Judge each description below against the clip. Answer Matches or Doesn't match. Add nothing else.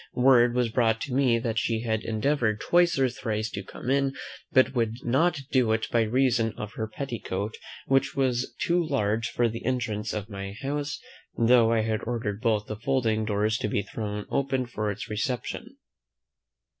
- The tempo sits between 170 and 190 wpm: Matches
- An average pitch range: Matches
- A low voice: Matches